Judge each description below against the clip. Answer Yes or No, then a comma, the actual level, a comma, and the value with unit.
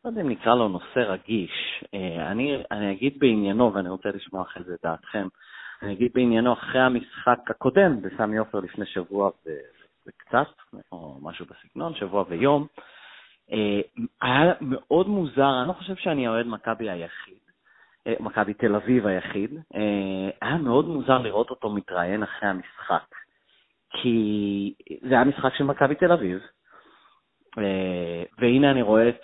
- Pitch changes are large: No, average, 4.6 semitones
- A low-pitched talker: Yes, low, 110 Hz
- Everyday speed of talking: Yes, average, 140 wpm